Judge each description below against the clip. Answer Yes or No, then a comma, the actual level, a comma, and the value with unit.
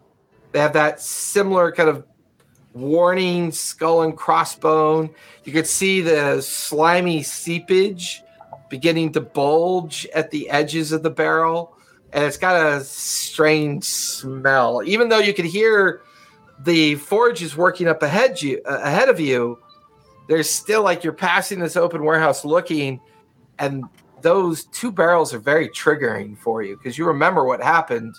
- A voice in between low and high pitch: Yes, medium, 160 Hz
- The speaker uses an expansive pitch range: No, average, 3.2 semitones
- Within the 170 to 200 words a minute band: No, average, 145 wpm